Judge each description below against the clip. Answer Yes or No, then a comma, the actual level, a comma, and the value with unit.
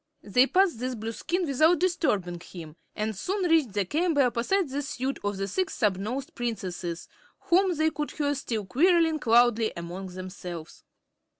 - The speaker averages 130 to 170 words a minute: Yes, average, 155 wpm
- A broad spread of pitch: Yes, wide, 8.3 semitones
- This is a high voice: Yes, high, 245 Hz